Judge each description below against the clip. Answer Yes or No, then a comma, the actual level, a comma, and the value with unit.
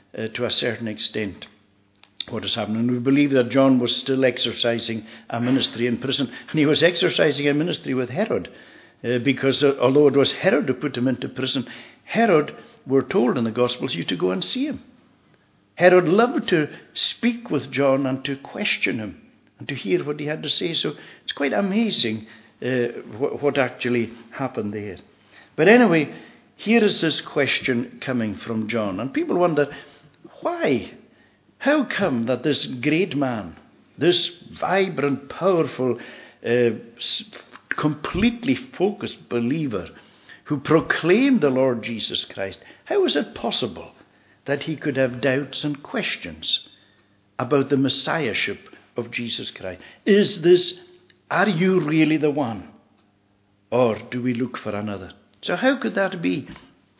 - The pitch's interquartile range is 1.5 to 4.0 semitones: No, wide, 5.6 semitones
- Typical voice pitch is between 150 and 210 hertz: No, low, 135 Hz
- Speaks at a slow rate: No, average, 155 wpm